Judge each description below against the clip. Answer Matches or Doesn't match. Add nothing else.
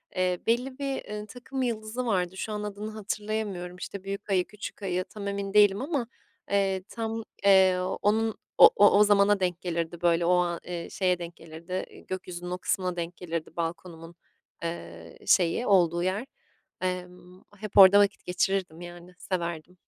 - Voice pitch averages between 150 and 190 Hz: Matches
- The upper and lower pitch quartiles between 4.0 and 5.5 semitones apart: Doesn't match